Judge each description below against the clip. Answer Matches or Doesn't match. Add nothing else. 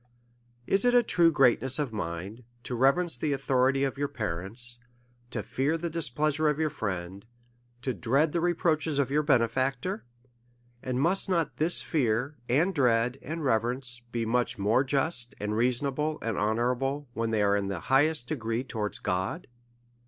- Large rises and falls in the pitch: Doesn't match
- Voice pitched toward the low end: Matches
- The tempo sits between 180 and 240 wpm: Doesn't match